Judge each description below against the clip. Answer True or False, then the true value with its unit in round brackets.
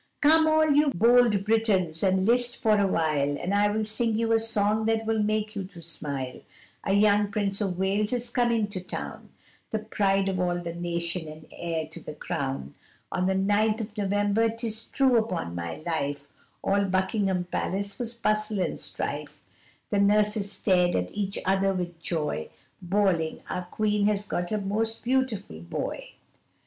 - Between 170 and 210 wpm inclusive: True (175 wpm)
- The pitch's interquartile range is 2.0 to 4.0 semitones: True (3.7 semitones)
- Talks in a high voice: True (200 Hz)